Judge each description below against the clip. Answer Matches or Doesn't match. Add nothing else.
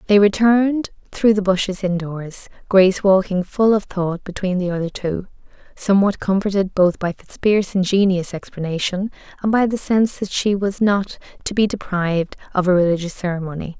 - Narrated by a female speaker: Matches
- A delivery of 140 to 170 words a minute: Matches